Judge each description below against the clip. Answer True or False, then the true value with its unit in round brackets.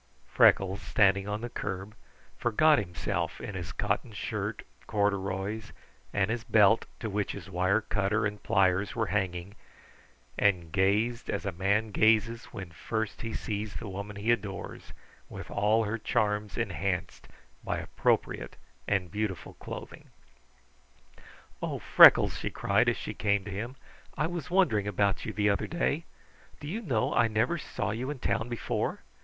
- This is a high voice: False (105 Hz)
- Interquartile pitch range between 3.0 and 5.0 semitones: False (2.6 semitones)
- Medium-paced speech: True (155 wpm)